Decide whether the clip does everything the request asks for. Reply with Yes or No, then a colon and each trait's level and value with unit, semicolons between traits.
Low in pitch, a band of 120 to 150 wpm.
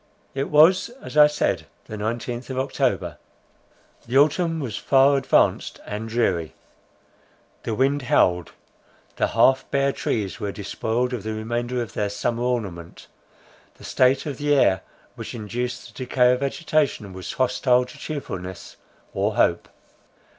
Yes: low, 125 Hz; average, 145 wpm